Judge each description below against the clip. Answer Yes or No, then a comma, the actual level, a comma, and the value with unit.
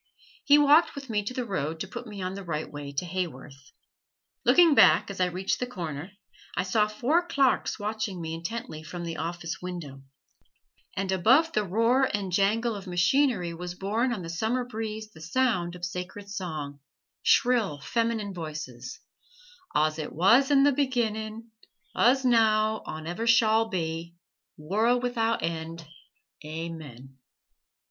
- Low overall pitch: No, high, 195 Hz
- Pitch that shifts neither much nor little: No, wide, 5.8 semitones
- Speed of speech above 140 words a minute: Yes, average, 155 wpm